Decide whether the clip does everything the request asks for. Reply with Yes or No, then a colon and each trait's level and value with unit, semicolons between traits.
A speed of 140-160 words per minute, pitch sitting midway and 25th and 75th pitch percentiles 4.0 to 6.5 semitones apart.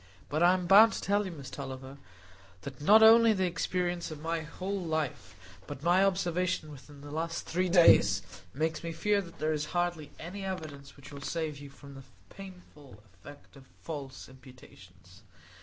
No: average, 175 wpm; medium, 160 Hz; average, 4.4 semitones